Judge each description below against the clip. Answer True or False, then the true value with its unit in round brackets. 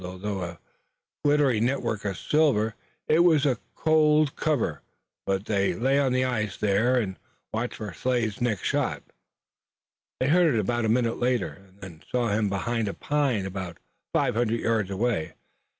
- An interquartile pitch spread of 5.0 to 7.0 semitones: False (4.5 semitones)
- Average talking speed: True (160 wpm)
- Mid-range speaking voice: False (115 Hz)